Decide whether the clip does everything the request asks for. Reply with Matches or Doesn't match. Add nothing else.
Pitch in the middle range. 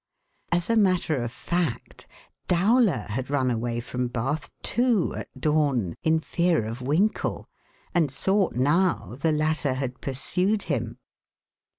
Matches